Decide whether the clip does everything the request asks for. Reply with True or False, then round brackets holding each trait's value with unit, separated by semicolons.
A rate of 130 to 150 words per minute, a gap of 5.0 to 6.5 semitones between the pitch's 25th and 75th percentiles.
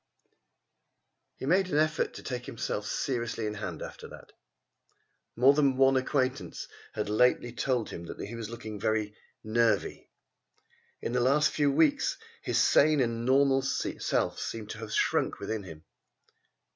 False (145 wpm; 3.9 semitones)